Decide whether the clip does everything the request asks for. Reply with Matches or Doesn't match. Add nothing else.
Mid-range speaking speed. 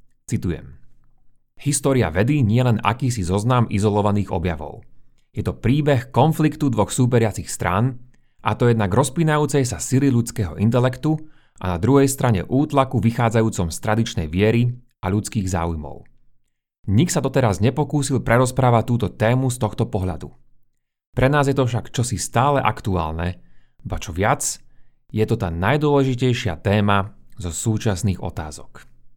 Matches